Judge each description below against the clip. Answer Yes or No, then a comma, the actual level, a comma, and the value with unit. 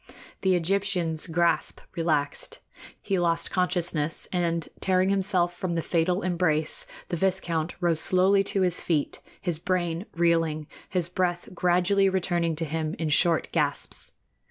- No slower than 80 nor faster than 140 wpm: Yes, slow, 135 wpm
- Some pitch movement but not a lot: No, narrow, 2.1 semitones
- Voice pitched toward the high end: No, medium, 175 Hz